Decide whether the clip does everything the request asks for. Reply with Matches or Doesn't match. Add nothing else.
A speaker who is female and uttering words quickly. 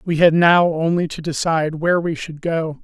Doesn't match